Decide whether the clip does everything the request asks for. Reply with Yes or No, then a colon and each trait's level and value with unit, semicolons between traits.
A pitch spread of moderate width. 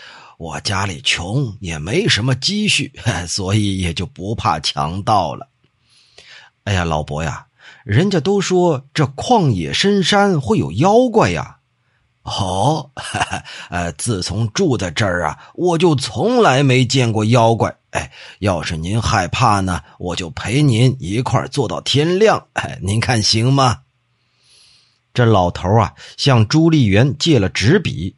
No: wide, 6.0 semitones